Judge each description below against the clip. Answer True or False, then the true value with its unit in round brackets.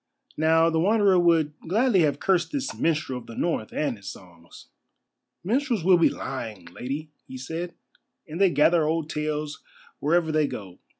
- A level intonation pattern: False (3.7 semitones)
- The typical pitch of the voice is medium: True (160 Hz)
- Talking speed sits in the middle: True (165 wpm)